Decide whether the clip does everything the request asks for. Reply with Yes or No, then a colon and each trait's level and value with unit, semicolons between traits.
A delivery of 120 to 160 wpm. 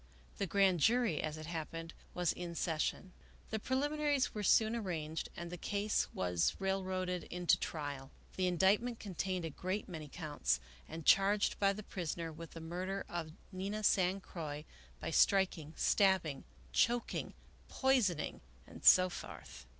Yes: average, 140 wpm